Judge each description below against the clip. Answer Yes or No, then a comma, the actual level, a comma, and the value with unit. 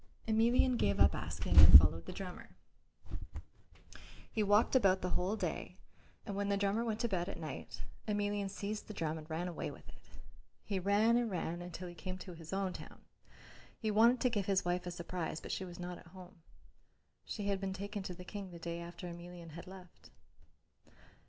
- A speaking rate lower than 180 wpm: No, average, 195 wpm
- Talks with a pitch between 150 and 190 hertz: Yes, medium, 185 Hz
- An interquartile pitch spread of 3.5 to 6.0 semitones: No, average, 2.9 semitones